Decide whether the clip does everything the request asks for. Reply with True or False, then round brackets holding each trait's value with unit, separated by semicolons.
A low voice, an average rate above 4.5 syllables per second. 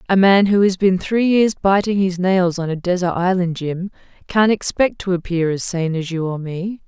False (185 Hz; 4.8 syllables/s)